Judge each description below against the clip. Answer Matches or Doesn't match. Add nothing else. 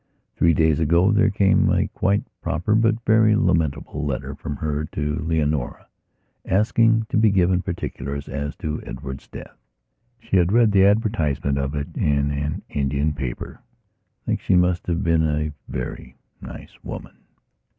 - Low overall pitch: Matches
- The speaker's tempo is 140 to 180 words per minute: Matches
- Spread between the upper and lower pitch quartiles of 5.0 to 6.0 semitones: Matches